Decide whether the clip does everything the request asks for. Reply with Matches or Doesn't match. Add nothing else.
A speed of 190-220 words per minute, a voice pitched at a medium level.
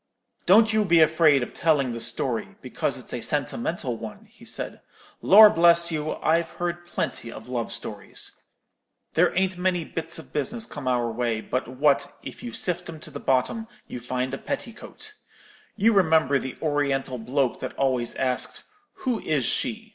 Doesn't match